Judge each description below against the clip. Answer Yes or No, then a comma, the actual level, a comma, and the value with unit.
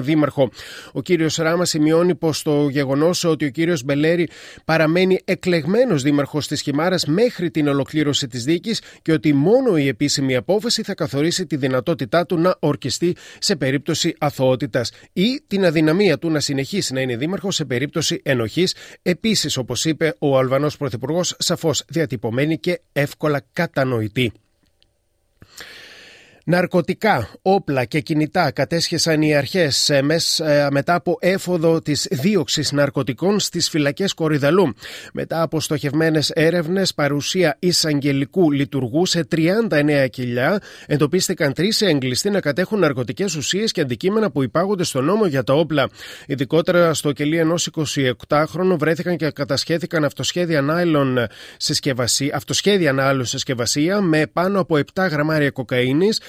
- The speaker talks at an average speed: Yes, average, 130 wpm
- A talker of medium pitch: Yes, medium, 155 Hz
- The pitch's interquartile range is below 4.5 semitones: Yes, average, 3.8 semitones